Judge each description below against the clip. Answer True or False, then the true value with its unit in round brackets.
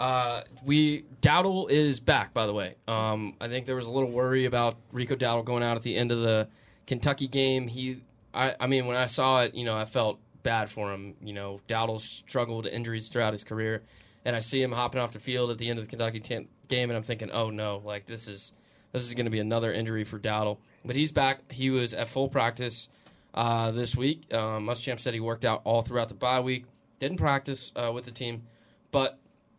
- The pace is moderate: False (225 wpm)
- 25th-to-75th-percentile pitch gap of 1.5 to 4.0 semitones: True (2.4 semitones)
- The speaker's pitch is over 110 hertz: True (120 Hz)